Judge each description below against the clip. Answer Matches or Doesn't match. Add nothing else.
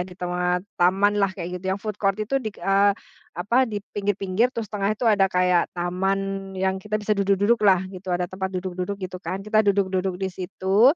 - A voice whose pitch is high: Matches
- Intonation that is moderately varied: Doesn't match